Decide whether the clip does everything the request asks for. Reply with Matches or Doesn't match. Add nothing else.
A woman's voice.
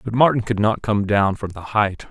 Doesn't match